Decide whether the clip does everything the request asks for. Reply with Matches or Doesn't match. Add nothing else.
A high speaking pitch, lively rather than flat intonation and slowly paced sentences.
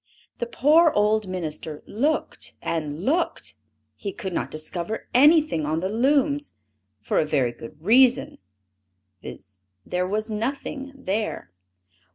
Matches